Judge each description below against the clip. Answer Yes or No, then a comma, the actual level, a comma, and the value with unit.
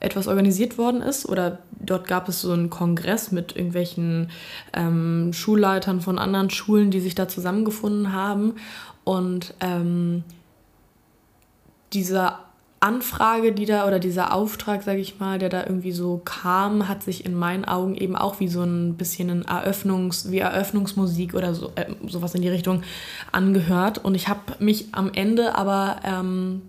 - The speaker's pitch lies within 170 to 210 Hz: Yes, high, 190 Hz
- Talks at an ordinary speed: Yes, average, 160 wpm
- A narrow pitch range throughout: Yes, narrow, 1.8 semitones